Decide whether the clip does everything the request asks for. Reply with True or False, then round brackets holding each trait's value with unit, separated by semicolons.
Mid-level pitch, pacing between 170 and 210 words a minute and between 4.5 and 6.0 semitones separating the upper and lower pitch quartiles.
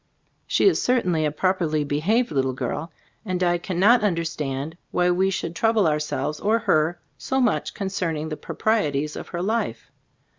True (175 Hz; 175 wpm; 5.0 semitones)